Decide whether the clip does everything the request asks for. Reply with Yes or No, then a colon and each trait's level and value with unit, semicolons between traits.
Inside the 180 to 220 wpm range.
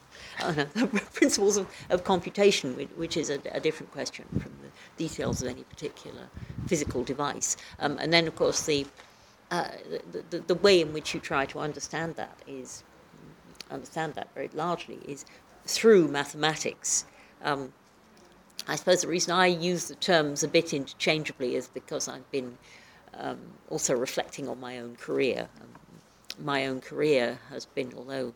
No: average, 165 wpm